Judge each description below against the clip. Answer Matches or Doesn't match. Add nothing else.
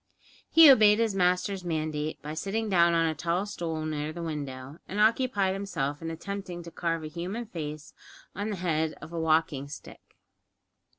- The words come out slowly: Doesn't match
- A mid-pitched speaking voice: Matches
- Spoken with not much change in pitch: Doesn't match